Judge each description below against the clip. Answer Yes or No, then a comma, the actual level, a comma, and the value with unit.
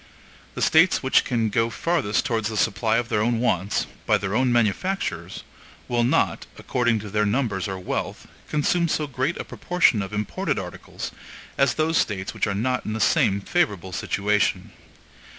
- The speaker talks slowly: No, average, 170 wpm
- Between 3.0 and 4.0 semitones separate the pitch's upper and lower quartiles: No, average, 4.4 semitones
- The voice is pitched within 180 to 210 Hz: No, low, 115 Hz